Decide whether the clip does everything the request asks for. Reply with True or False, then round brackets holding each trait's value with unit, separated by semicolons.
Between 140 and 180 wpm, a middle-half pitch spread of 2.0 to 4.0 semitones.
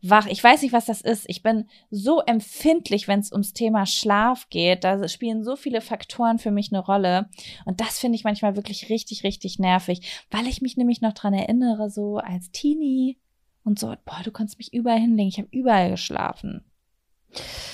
False (190 wpm; 2.8 semitones)